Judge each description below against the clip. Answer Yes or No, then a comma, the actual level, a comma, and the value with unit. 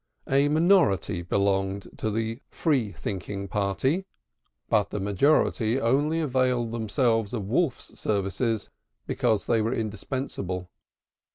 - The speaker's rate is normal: No, slow, 110 wpm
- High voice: No, low, 110 Hz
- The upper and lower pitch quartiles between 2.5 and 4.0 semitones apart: No, average, 4.9 semitones